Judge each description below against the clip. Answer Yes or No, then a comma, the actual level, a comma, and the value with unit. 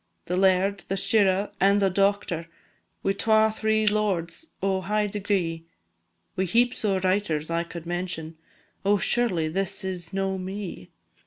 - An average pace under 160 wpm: Yes, average, 145 wpm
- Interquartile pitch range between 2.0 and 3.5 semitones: Yes, average, 2.7 semitones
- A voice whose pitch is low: No, high, 195 Hz